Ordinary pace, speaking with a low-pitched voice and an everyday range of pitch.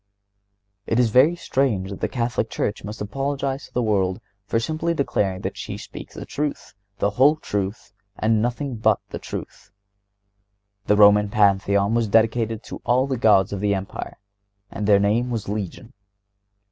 Yes: average, 165 wpm; low, 110 Hz; average, 3.7 semitones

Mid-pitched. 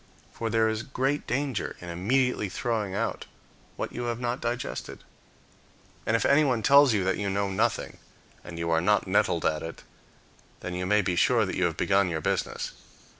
No: low, 110 Hz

